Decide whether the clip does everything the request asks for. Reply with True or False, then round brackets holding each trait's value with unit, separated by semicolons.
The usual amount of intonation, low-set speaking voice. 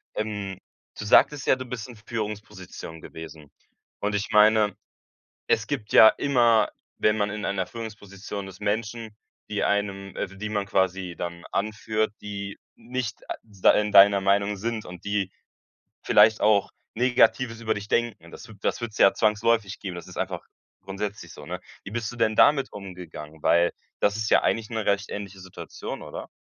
False (2.2 semitones; 105 Hz)